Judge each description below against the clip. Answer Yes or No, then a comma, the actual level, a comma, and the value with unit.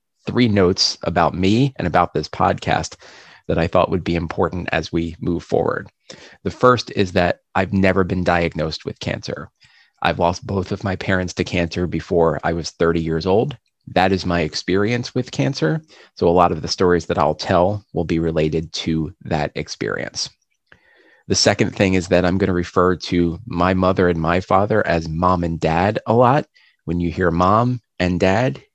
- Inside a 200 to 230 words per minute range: No, average, 190 wpm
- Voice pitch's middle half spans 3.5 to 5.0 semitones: No, average, 2.7 semitones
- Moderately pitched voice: No, very low, 90 Hz